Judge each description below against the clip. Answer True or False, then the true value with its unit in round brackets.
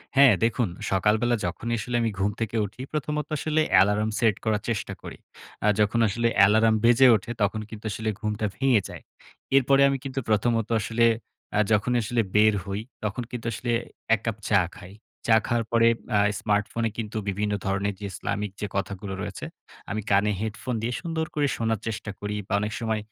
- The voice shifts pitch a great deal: False (2.4 semitones)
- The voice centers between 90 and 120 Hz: True (110 Hz)